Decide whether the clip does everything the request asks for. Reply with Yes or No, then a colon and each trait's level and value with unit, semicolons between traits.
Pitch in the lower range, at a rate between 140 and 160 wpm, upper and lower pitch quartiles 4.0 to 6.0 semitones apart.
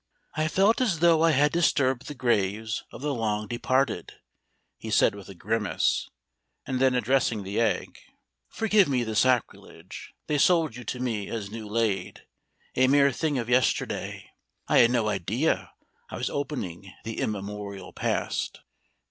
Yes: low, 120 Hz; average, 155 wpm; average, 5.0 semitones